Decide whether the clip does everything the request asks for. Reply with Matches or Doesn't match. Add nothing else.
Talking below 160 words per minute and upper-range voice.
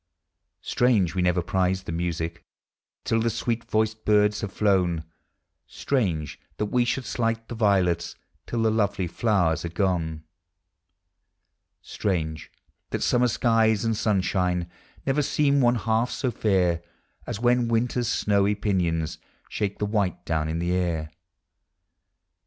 Doesn't match